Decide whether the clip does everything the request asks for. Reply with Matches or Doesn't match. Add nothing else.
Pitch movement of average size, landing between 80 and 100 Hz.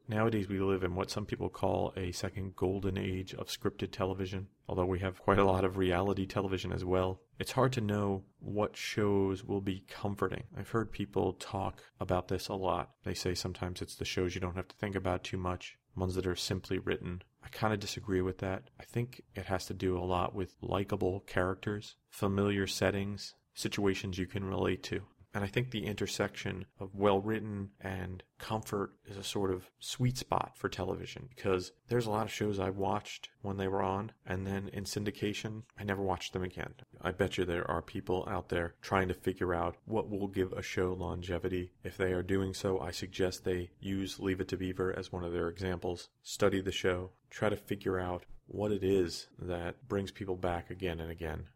Doesn't match